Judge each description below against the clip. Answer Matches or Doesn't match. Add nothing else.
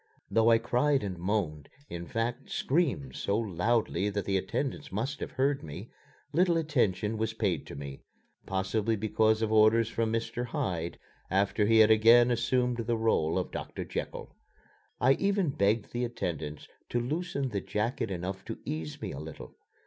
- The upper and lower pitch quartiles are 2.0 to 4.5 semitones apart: Matches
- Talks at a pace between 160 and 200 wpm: Matches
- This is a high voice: Doesn't match